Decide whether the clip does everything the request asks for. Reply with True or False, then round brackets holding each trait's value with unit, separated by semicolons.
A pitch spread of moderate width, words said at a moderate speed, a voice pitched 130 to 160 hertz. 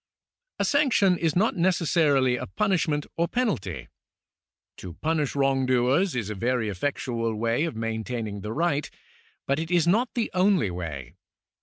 False (7.4 semitones; 150 wpm; 140 Hz)